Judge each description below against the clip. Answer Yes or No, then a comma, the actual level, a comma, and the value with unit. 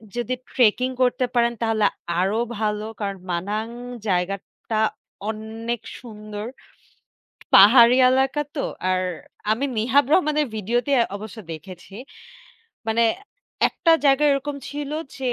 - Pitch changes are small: No, average, 3.8 semitones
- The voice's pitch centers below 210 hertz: No, high, 225 Hz